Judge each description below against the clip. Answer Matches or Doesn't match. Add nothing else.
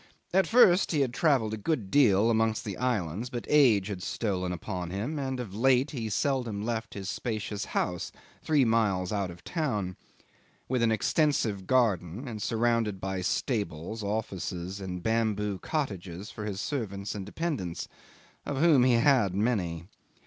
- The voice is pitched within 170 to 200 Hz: Doesn't match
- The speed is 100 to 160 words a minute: Matches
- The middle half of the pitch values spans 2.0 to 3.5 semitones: Doesn't match